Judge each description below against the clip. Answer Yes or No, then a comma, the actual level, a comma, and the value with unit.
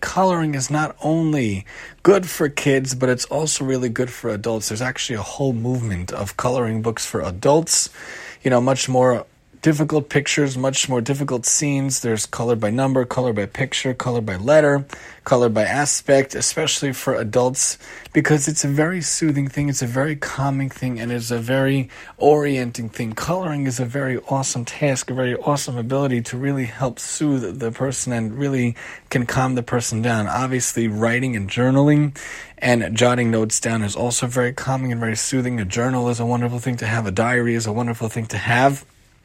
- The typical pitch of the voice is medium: No, low, 125 Hz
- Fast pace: No, average, 185 wpm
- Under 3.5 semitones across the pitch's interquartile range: Yes, average, 2.9 semitones